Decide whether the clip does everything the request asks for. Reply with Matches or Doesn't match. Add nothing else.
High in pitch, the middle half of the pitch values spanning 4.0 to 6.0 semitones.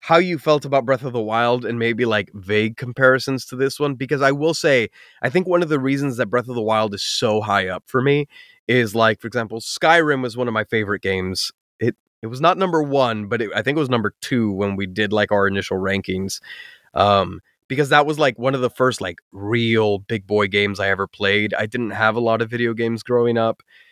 Doesn't match